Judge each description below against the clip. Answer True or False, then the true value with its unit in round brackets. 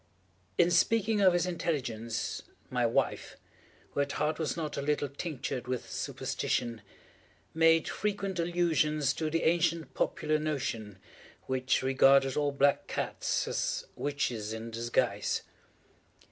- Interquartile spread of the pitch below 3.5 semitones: False (4.3 semitones)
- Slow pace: True (125 wpm)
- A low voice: False (150 Hz)